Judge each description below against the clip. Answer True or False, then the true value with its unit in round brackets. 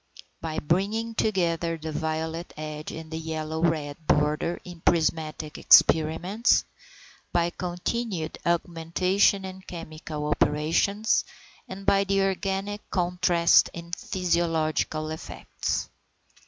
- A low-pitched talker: False (170 Hz)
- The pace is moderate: False (100 wpm)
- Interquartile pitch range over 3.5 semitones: False (3.0 semitones)